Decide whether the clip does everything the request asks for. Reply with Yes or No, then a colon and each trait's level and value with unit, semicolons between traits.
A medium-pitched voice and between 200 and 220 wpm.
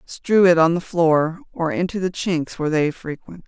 Yes: medium, 170 Hz; fast, 205 wpm